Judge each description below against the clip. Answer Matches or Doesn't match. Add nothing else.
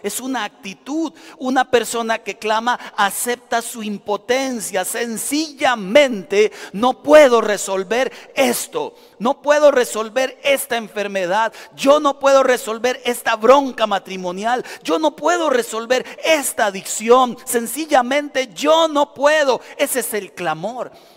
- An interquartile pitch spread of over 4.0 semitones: Matches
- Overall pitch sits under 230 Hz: Doesn't match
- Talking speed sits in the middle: Doesn't match